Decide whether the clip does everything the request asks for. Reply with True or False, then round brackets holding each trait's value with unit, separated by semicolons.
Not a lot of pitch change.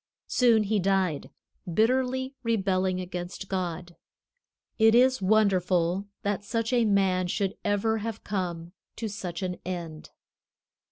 False (3.5 semitones)